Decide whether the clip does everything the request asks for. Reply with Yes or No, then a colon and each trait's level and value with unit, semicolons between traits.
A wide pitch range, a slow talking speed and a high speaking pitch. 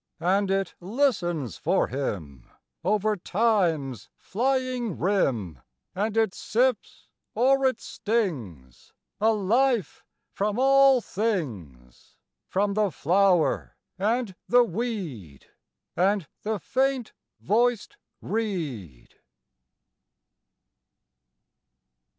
Yes: wide, 7.1 semitones; slow, 85 wpm; high, 200 Hz